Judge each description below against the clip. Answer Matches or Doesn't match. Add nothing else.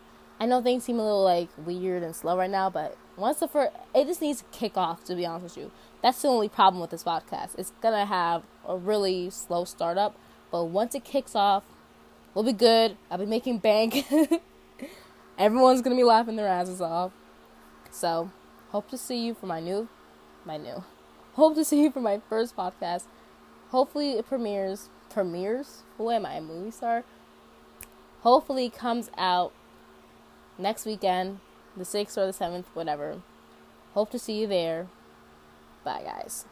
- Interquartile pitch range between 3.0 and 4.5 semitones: Doesn't match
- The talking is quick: Doesn't match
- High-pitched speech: Matches